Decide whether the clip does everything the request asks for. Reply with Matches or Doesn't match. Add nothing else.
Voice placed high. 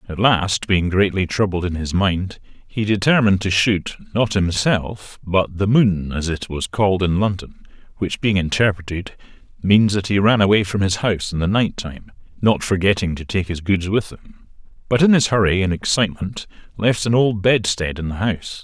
Doesn't match